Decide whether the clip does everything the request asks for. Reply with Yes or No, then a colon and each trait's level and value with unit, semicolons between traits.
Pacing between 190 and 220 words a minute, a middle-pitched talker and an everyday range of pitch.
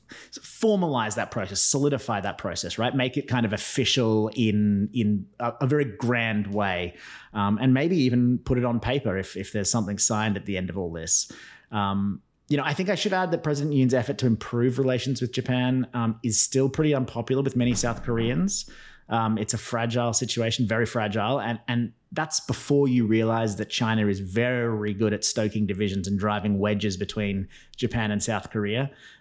No: average, 195 wpm; low, 115 Hz; average, 3.6 semitones